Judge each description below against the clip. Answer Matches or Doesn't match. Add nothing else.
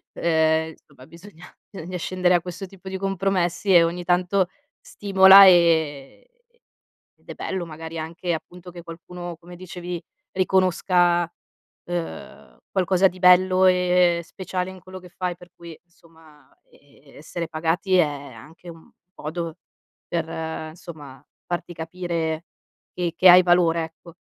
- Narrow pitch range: Matches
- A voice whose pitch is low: Doesn't match